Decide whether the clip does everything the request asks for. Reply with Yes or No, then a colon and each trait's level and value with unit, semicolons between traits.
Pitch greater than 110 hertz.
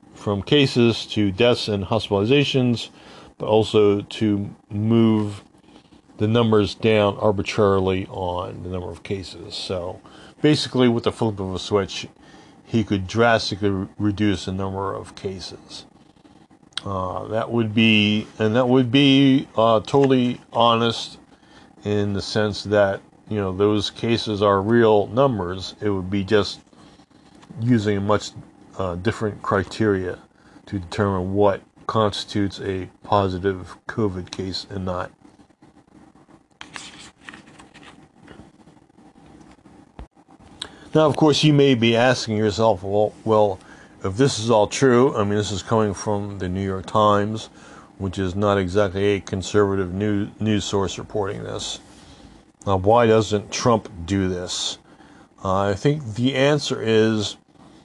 No: low, 105 Hz